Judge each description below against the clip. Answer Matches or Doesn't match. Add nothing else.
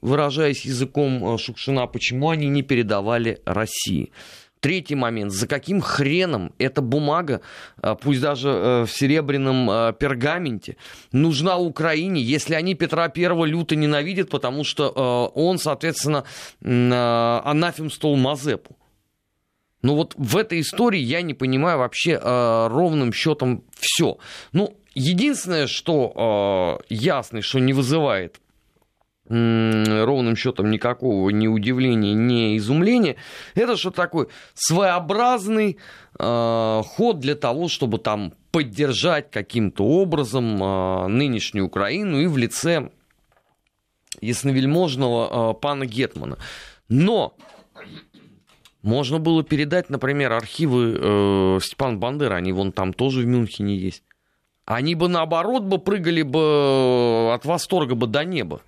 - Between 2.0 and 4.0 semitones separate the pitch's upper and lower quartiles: Doesn't match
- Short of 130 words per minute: Matches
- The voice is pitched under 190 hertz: Matches